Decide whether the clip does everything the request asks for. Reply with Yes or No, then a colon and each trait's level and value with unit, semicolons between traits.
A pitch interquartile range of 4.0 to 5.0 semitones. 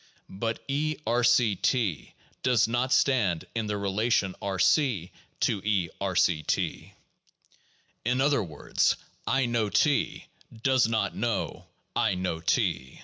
Yes: average, 4.5 semitones